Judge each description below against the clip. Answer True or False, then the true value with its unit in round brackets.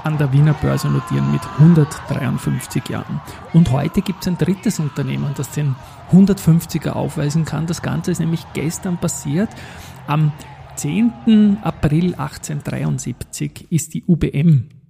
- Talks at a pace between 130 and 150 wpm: True (135 wpm)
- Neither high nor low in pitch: True (155 Hz)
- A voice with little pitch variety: False (3.1 semitones)